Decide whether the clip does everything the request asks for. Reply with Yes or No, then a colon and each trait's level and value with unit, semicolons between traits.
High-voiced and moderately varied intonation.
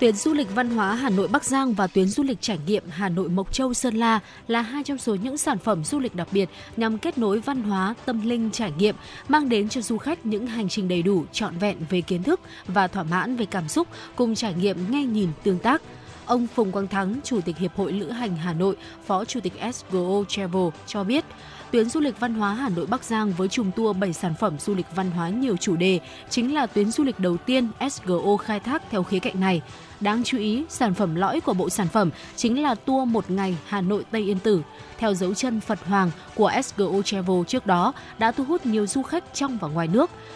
Yes: high, 210 Hz; average, 4.4 semitones